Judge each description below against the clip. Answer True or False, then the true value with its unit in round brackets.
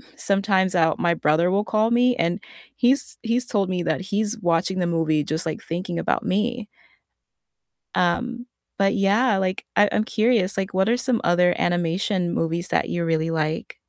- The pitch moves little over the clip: False (4.0 semitones)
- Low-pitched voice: False (190 Hz)